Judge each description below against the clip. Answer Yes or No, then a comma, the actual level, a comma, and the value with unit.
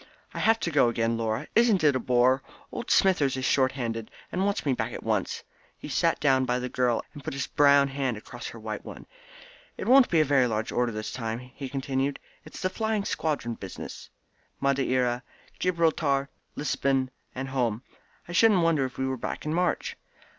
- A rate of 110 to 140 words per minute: No, average, 195 wpm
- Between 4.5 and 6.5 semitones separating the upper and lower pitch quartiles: No, average, 3.8 semitones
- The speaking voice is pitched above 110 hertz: Yes, low, 135 Hz